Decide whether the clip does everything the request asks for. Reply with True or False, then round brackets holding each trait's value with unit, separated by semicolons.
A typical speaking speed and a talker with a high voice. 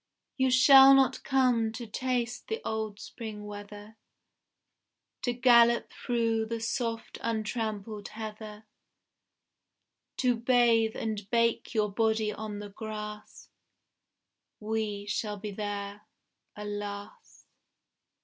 False (100 wpm; 220 Hz)